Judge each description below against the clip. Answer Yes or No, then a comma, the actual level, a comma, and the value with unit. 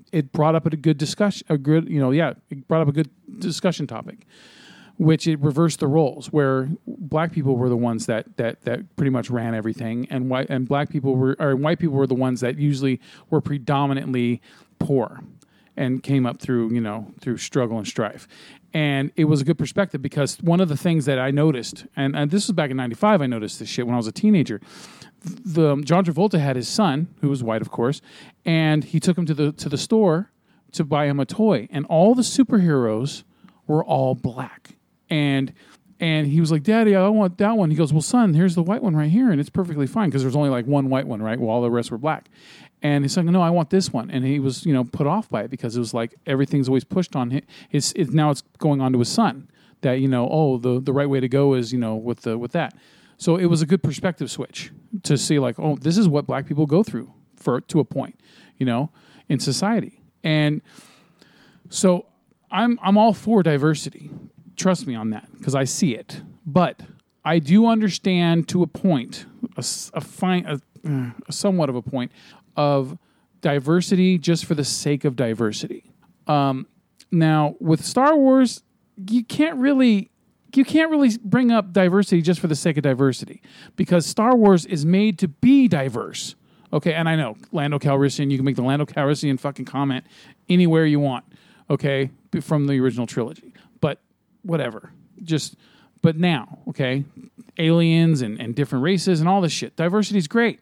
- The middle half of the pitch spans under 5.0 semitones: No, wide, 5.4 semitones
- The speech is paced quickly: Yes, fast, 210 wpm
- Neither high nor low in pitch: Yes, medium, 155 Hz